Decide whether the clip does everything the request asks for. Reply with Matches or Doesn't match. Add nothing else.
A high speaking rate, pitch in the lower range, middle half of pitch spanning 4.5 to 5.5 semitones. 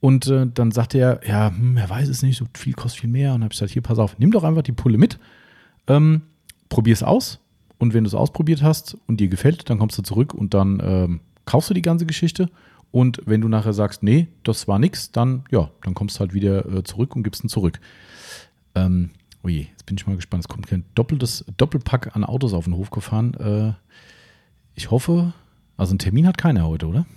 Matches